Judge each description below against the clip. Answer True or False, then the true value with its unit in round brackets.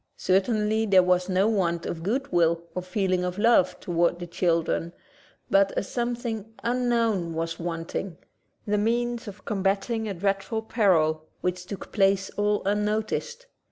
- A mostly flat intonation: False (3.8 semitones)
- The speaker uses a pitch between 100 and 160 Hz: False (195 Hz)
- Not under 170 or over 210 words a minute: False (145 wpm)